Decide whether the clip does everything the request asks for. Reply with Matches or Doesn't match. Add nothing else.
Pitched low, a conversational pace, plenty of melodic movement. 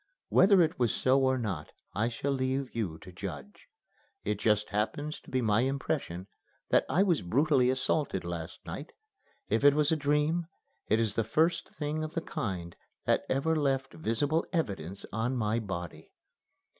Matches